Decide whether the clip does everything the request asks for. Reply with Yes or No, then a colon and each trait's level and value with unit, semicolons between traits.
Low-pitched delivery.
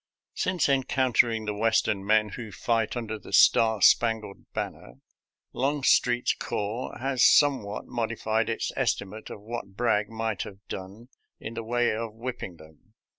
Yes: low, 115 Hz